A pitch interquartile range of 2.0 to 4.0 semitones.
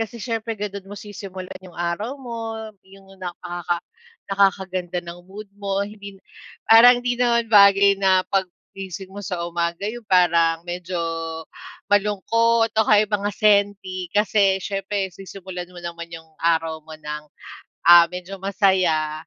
Yes: average, 2.8 semitones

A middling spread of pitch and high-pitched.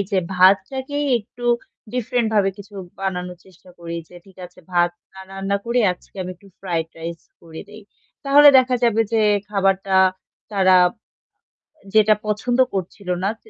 Yes: average, 4.1 semitones; high, 195 Hz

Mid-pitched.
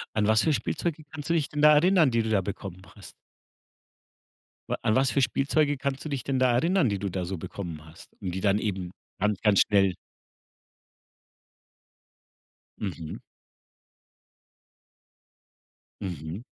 No: low, 110 Hz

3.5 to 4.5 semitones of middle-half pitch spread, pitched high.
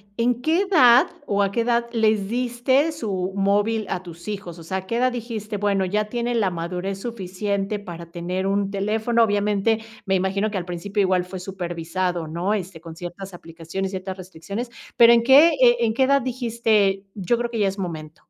Yes: average, 4.0 semitones; high, 200 Hz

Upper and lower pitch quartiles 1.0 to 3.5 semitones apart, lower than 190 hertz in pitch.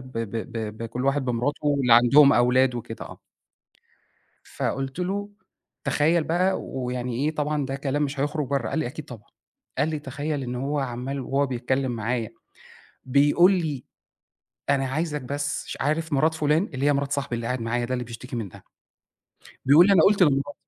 Yes: average, 3.1 semitones; low, 135 Hz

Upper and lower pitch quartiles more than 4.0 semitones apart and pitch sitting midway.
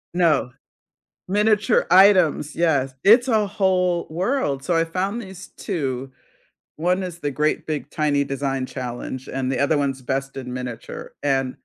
Yes: wide, 5.5 semitones; medium, 150 Hz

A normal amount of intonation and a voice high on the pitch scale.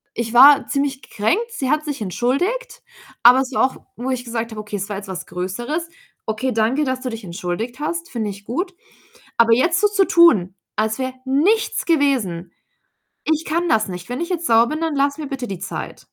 No: wide, 6.1 semitones; very high, 260 Hz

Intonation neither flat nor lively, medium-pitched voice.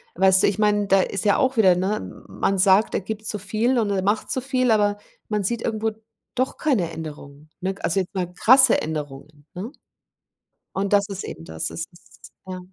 No: average, 3.4 semitones; high, 200 Hz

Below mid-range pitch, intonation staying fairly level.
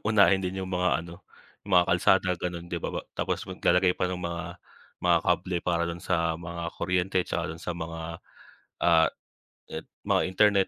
Yes: very low, 90 Hz; narrow, 1.6 semitones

